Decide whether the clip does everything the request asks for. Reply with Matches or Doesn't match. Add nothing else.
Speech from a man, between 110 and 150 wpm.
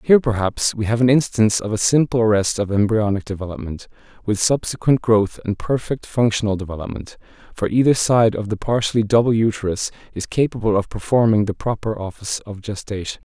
Doesn't match